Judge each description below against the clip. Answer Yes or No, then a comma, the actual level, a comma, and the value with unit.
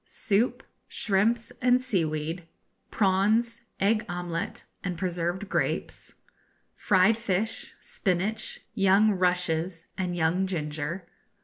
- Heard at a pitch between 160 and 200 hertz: Yes, high, 190 Hz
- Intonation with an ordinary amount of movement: Yes, average, 3.5 semitones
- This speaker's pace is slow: Yes, slow, 95 wpm